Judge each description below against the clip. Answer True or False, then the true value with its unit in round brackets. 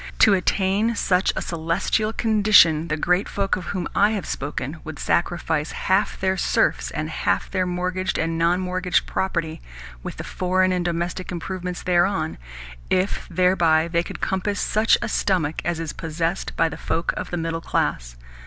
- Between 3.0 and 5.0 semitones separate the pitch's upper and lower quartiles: False (2.4 semitones)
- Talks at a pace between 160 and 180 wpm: True (170 wpm)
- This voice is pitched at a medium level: True (180 Hz)